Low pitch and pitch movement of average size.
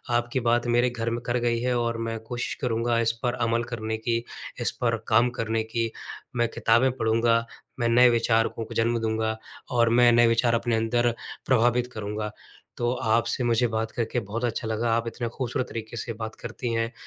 No: low, 115 Hz; narrow, 1.0 semitones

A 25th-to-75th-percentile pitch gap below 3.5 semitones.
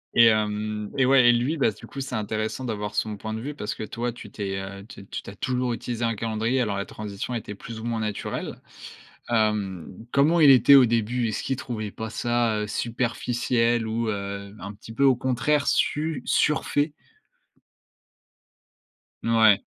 Yes: average, 2.8 semitones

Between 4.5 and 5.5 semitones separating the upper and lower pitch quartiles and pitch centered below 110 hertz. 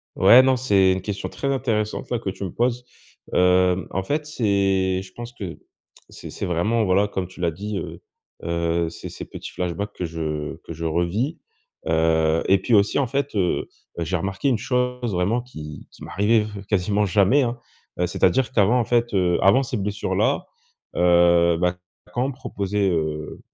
Yes: average, 5.2 semitones; very low, 95 Hz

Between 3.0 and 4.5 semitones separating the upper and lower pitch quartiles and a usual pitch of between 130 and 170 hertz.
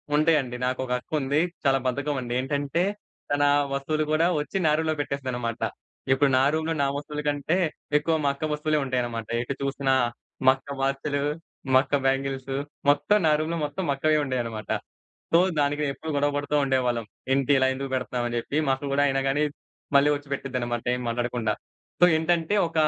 No: narrow, 2.4 semitones; medium, 140 Hz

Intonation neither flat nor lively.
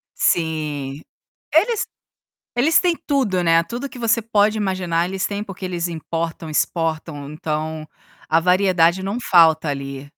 Yes: average, 4.2 semitones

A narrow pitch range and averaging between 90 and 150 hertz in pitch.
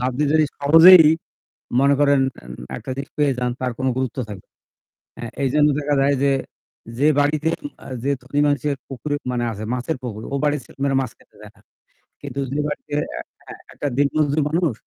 Yes: narrow, 2.3 semitones; medium, 140 Hz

